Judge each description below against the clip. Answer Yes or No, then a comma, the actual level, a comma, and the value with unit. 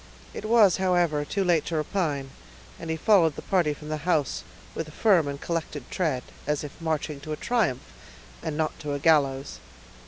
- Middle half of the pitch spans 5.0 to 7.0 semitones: No, average, 3.2 semitones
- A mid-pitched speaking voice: Yes, medium, 155 Hz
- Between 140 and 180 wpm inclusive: No, average, 190 wpm